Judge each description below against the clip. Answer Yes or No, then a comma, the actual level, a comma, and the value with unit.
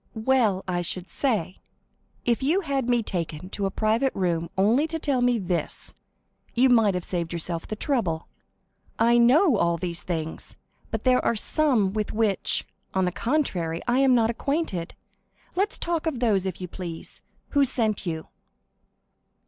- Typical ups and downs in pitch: No, wide, 6.3 semitones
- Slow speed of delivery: No, average, 165 wpm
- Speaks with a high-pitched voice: Yes, high, 220 Hz